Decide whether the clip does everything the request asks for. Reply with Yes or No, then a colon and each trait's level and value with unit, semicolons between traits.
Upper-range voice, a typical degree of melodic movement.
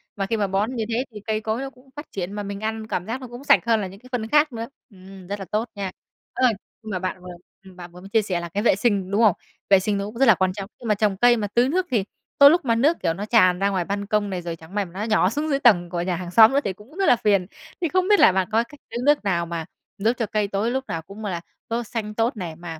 Yes: high, 210 Hz; average, 3.8 semitones